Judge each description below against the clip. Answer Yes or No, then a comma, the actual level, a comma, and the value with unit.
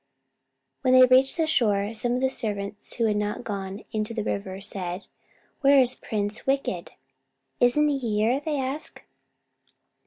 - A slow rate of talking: No, average, 155 wpm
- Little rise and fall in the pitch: No, average, 4.2 semitones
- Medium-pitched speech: No, high, 230 Hz